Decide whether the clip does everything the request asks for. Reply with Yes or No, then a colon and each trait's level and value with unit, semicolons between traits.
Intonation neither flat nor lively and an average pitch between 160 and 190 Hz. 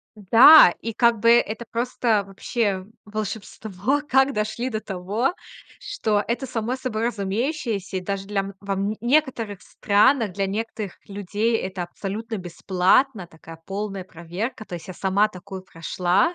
No: average, 3.5 semitones; high, 210 Hz